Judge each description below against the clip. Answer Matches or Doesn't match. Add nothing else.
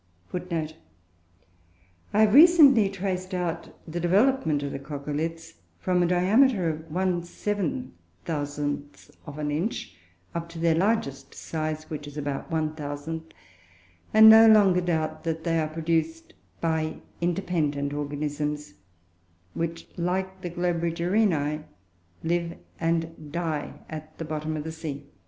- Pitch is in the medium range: Matches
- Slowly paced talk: Matches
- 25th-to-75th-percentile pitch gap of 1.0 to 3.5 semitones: Matches